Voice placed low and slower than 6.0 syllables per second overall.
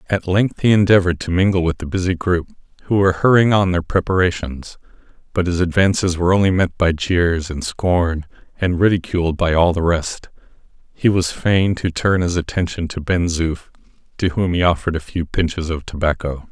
Yes: very low, 90 Hz; 5.4 syllables/s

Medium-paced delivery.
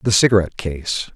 Yes: average, 155 wpm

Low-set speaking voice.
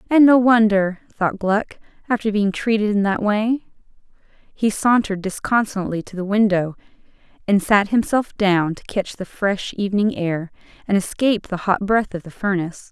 No: high, 205 Hz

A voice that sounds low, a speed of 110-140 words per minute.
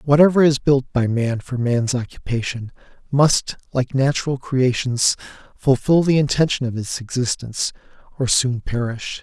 Yes: low, 130 Hz; slow, 135 wpm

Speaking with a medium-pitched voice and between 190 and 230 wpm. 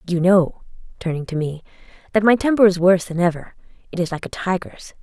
Yes: medium, 180 Hz; fast, 205 wpm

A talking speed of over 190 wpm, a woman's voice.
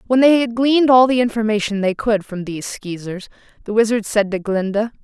Yes: fast, 205 wpm; female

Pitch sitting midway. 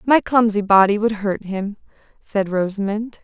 No: high, 210 Hz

